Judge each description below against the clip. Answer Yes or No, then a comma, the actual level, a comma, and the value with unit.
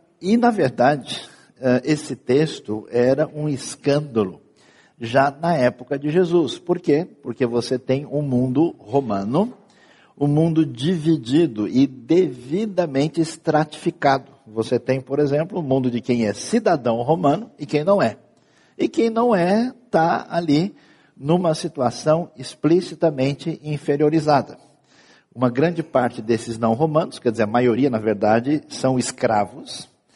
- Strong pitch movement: No, average, 4.7 semitones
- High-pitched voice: No, medium, 145 Hz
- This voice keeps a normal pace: Yes, average, 130 wpm